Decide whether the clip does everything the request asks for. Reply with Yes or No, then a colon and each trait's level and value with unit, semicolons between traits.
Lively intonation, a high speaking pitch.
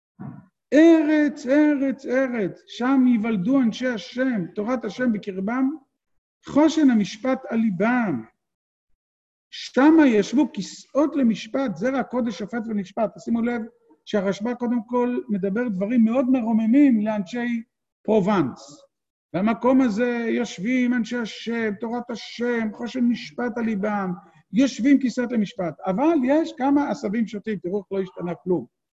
No: average, 3.7 semitones; high, 240 Hz